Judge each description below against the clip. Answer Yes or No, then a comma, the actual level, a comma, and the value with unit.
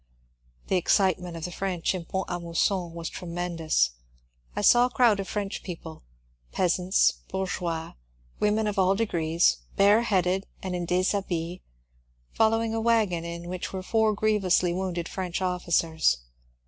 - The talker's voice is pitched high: No, medium, 180 Hz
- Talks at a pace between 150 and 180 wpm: Yes, average, 155 wpm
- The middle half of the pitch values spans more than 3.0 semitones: No, average, 2.7 semitones